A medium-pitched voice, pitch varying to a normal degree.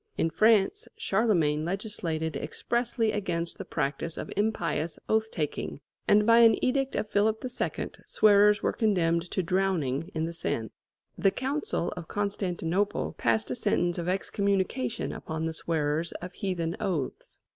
Yes: medium, 180 Hz; average, 4.5 semitones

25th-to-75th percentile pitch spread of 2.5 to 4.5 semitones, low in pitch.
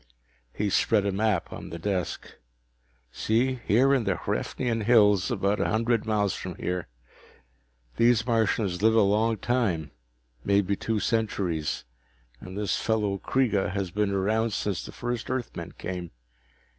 Yes: average, 2.8 semitones; low, 105 Hz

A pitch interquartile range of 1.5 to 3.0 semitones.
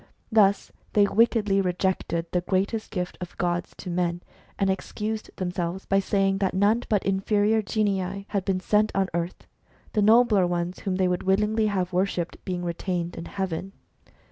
Yes: narrow, 2.4 semitones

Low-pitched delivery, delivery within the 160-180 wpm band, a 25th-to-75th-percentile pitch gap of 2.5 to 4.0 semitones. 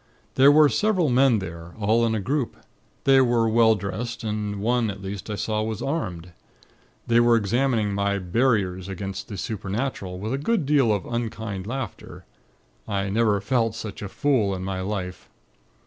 Yes: low, 110 Hz; average, 170 wpm; average, 3.6 semitones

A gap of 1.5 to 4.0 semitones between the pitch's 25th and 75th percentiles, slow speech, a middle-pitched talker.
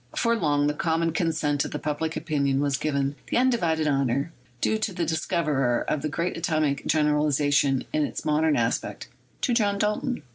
No: average, 2.7 semitones; average, 175 wpm; medium, 155 Hz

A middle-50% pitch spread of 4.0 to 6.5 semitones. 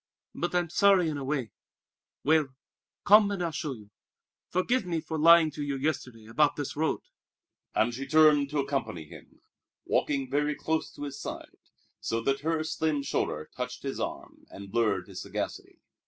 No: average, 3.3 semitones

